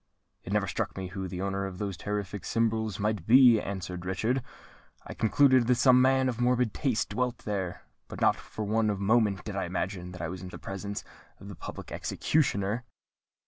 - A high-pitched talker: No, low, 105 Hz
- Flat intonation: No, average, 3.7 semitones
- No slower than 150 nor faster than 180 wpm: No, average, 190 wpm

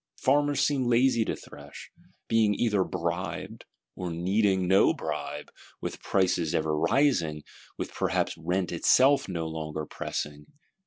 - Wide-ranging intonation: Yes, wide, 6.2 semitones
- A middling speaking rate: No, slow, 125 wpm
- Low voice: Yes, very low, 90 Hz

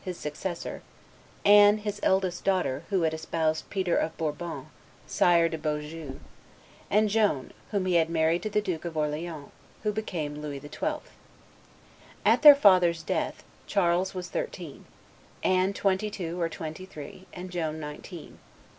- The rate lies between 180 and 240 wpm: No, average, 145 wpm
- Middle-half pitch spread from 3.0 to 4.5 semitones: Yes, average, 3.3 semitones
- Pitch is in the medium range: Yes, medium, 175 Hz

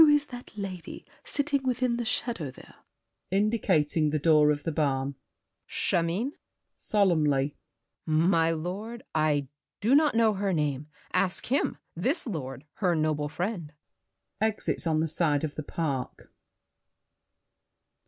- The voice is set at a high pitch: No, medium, 170 Hz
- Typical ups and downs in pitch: No, wide, 6.4 semitones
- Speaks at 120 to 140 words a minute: Yes, slow, 135 wpm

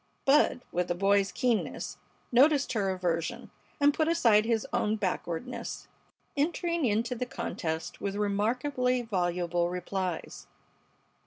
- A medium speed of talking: No, slow, 115 wpm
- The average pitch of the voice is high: Yes, high, 210 Hz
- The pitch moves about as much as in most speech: No, wide, 5.8 semitones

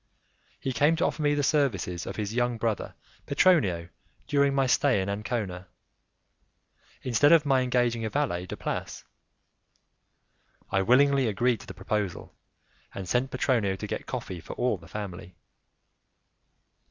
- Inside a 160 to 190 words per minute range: No, average, 145 wpm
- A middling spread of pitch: No, wide, 6.0 semitones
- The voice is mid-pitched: No, low, 120 Hz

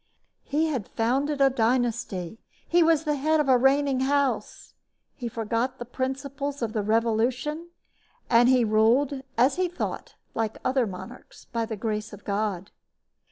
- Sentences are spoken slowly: No, average, 155 wpm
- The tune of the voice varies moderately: Yes, average, 3.9 semitones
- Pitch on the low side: No, very high, 255 Hz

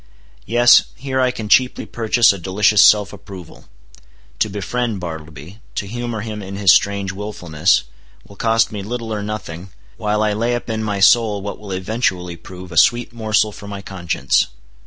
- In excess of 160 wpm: Yes, average, 175 wpm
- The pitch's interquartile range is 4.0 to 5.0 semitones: No, average, 3.1 semitones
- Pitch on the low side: Yes, low, 105 Hz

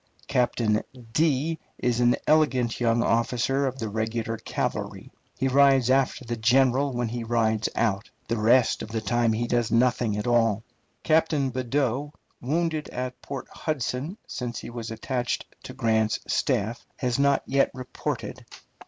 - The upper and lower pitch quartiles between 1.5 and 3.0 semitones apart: Yes, average, 2.7 semitones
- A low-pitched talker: Yes, low, 120 Hz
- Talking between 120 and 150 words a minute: Yes, average, 145 wpm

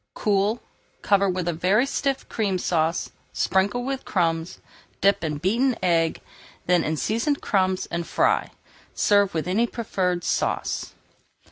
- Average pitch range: Yes, average, 4.1 semitones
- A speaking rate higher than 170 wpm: No, slow, 135 wpm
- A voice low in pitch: No, high, 190 Hz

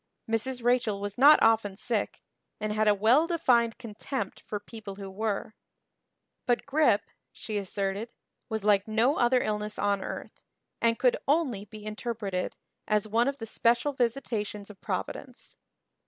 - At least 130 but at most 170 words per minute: Yes, average, 150 wpm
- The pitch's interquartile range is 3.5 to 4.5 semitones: No, average, 2.9 semitones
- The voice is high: Yes, high, 220 Hz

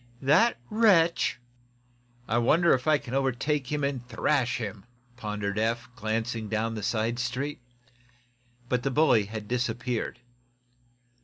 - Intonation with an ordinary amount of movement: Yes, average, 3.8 semitones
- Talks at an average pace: No, slow, 130 wpm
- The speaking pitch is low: Yes, low, 125 Hz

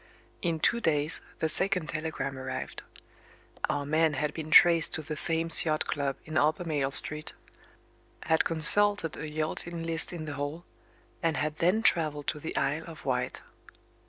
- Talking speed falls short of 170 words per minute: Yes, average, 160 wpm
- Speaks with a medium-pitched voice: Yes, medium, 155 Hz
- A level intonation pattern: Yes, narrow, 1.9 semitones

